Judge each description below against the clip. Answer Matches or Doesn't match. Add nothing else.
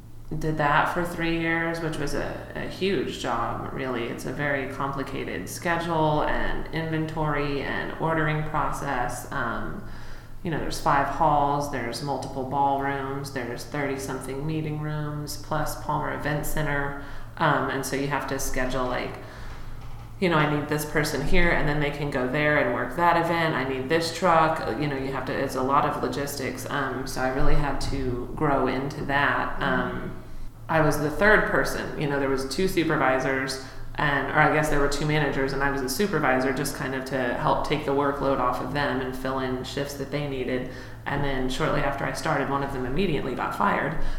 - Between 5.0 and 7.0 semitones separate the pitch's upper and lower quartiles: Doesn't match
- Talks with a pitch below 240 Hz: Matches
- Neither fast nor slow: Matches